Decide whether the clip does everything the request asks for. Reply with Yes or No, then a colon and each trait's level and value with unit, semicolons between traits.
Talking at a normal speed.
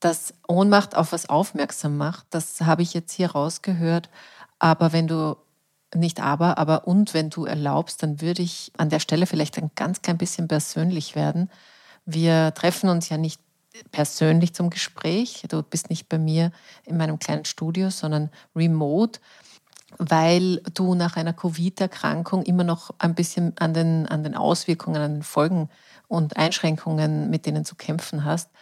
Yes: average, 165 wpm